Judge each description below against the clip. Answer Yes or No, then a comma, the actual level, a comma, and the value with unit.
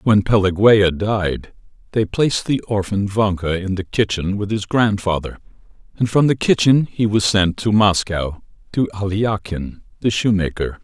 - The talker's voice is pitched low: Yes, low, 100 Hz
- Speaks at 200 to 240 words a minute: No, average, 150 wpm